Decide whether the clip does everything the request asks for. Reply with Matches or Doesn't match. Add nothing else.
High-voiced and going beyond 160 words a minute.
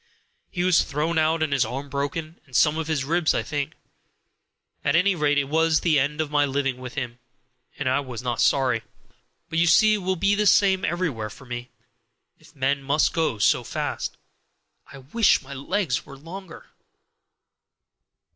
Doesn't match